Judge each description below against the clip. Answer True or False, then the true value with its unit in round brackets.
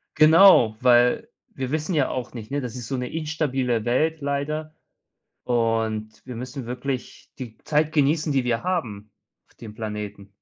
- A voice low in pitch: True (125 Hz)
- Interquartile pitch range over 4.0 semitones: True (4.8 semitones)